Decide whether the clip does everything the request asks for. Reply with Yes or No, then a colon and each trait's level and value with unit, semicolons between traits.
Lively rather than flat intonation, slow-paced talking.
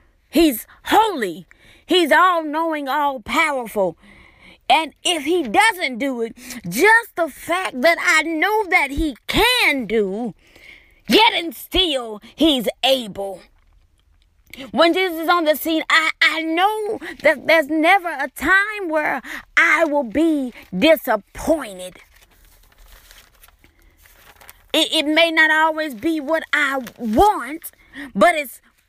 Yes: wide, 5.9 semitones; slow, 115 wpm